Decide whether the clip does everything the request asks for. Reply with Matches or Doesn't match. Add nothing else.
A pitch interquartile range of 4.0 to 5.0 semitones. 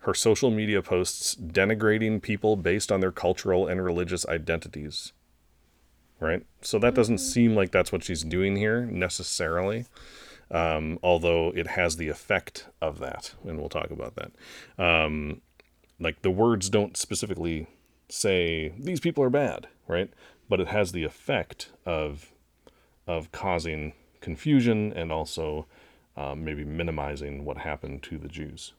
Matches